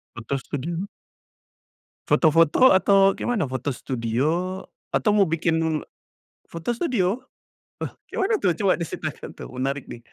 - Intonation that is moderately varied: No, wide, 5.8 semitones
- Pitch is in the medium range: Yes, medium, 165 Hz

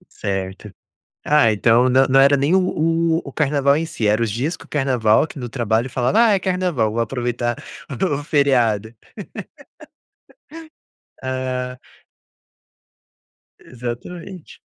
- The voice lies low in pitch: Yes, low, 130 Hz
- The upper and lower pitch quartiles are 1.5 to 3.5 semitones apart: No, average, 3.9 semitones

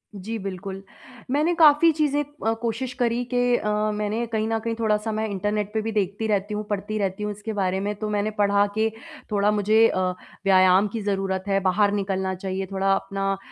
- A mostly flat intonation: Yes, narrow, 2.3 semitones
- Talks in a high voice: Yes, high, 210 Hz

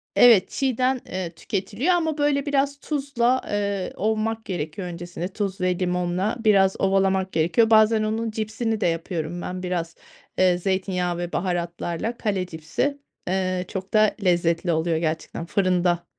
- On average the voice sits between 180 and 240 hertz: Yes, high, 190 Hz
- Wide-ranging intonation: No, average, 4.0 semitones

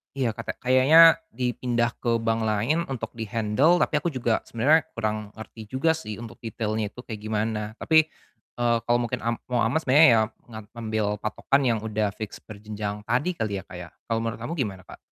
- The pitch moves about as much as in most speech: Yes, average, 3.2 semitones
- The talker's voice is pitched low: Yes, low, 115 Hz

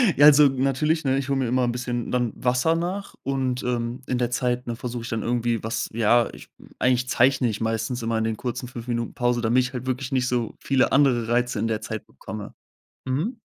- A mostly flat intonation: Yes, narrow, 2.0 semitones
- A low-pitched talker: Yes, low, 125 Hz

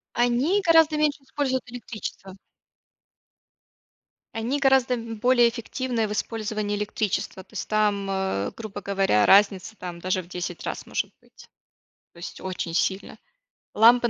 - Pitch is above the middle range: Yes, high, 220 Hz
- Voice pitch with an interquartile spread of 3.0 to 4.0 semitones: No, average, 4.5 semitones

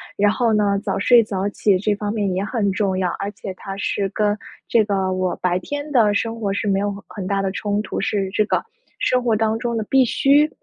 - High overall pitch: Yes, high, 205 Hz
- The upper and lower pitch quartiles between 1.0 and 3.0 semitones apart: Yes, narrow, 2.4 semitones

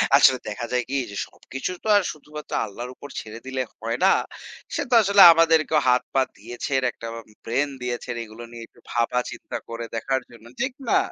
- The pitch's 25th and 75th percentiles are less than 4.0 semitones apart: No, average, 4.4 semitones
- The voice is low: Yes, low, 125 Hz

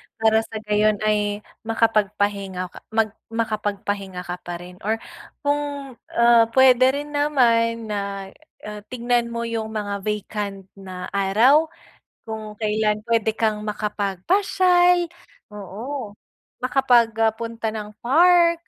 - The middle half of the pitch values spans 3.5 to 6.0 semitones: No, average, 3.0 semitones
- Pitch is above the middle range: Yes, high, 220 Hz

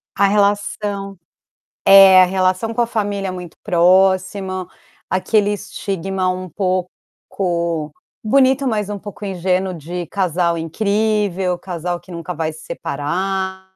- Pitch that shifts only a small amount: Yes, narrow, 2.2 semitones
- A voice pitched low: No, high, 190 Hz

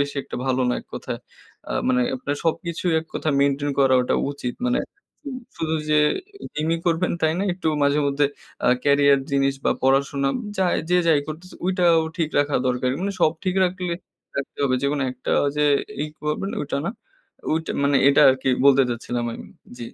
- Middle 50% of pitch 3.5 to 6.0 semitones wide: No, average, 3.0 semitones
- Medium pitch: Yes, medium, 145 Hz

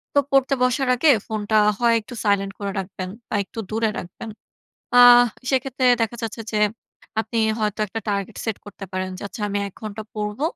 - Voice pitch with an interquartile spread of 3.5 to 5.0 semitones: No, average, 2.9 semitones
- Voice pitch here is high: Yes, high, 220 Hz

